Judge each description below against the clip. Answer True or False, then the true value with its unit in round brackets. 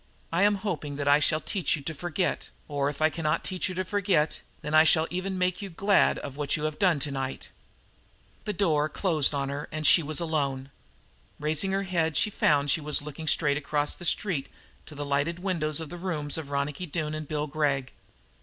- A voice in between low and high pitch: True (155 Hz)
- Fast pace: True (210 wpm)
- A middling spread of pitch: True (3.4 semitones)